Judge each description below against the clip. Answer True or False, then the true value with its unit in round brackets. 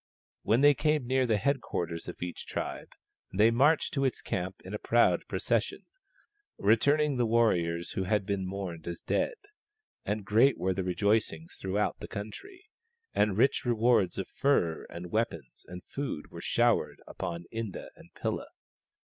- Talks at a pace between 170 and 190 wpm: False (160 wpm)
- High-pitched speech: False (105 Hz)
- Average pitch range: False (5.7 semitones)